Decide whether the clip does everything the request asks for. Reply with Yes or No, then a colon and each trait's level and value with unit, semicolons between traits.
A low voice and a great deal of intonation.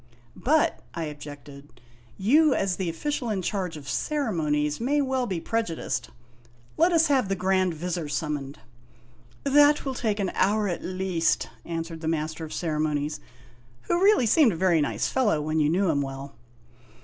No: medium, 180 Hz; wide, 7.5 semitones